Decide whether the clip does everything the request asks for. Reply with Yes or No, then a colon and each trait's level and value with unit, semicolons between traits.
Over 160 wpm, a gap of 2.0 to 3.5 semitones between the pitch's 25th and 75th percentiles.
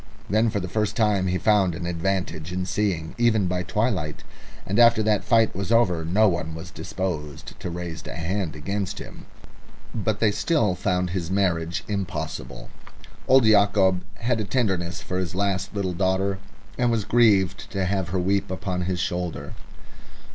Yes: average, 170 wpm; average, 3.0 semitones